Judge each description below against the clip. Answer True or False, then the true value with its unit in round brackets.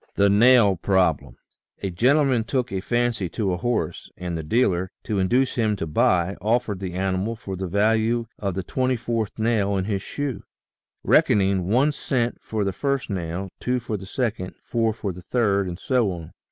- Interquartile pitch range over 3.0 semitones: True (4.1 semitones)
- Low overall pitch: True (105 Hz)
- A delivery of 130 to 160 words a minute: False (180 wpm)